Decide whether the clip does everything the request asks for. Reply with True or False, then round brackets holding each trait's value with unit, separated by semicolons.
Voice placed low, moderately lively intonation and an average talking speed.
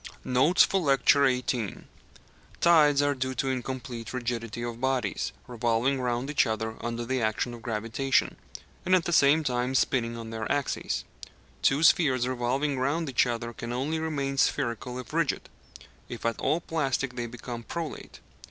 True (130 Hz; 3.0 semitones; 160 wpm)